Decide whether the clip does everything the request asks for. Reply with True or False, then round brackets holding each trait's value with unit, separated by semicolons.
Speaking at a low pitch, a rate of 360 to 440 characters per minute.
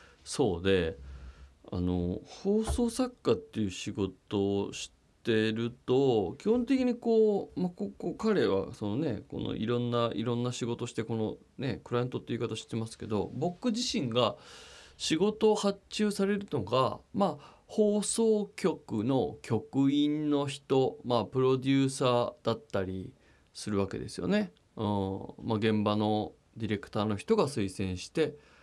False (120 Hz; 300 characters per minute)